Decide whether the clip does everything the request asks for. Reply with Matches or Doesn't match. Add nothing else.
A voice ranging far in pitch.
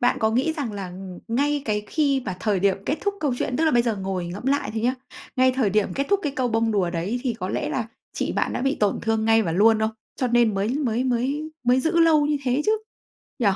Doesn't match